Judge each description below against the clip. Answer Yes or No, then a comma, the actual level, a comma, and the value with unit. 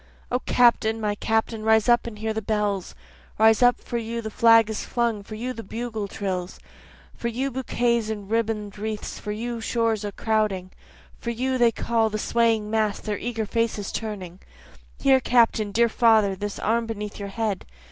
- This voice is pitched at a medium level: No, high, 220 Hz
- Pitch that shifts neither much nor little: No, narrow, 1.9 semitones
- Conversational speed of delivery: Yes, average, 185 wpm